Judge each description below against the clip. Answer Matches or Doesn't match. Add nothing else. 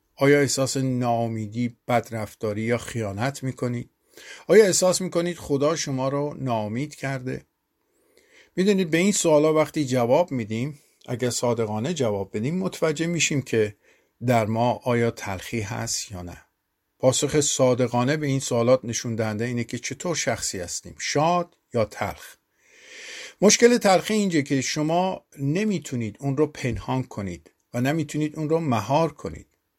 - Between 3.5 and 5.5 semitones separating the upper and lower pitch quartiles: Matches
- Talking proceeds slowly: Doesn't match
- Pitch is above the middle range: Doesn't match